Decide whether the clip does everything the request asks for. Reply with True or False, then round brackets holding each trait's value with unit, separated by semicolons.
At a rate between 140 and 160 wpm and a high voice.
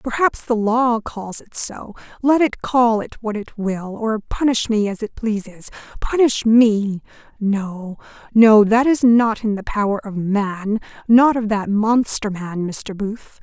True (145 wpm; 220 Hz)